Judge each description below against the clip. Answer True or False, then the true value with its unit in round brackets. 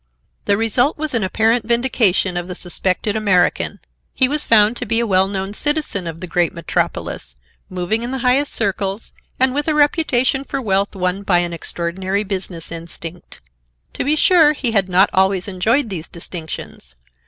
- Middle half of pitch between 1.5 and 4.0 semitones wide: False (5.4 semitones)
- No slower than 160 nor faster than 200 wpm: True (175 wpm)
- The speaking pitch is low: False (200 Hz)